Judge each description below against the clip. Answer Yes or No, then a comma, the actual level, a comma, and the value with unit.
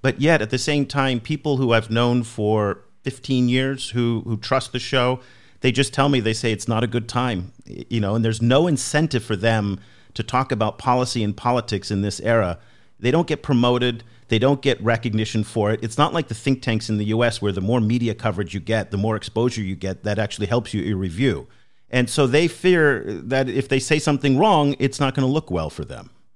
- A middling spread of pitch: Yes, average, 3.5 semitones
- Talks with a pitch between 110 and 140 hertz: Yes, low, 120 Hz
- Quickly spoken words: Yes, fast, 230 wpm